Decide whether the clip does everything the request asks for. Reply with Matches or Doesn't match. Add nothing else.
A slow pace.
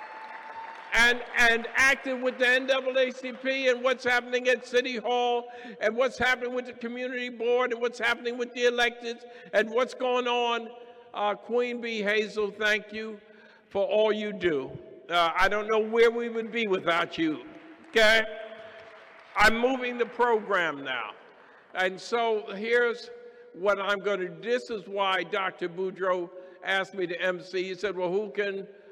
Doesn't match